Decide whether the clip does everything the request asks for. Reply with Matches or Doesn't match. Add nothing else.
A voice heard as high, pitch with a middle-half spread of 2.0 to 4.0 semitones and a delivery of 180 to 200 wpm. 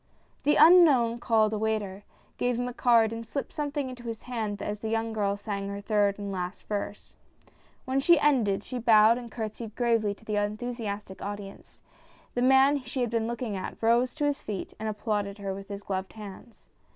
Matches